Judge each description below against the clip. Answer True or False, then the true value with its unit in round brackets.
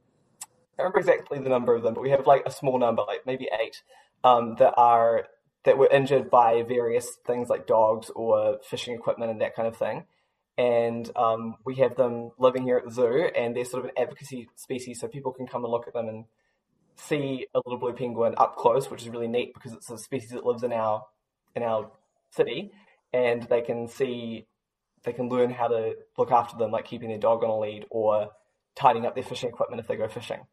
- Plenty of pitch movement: True (7.5 semitones)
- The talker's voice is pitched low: True (125 Hz)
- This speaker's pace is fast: True (220 wpm)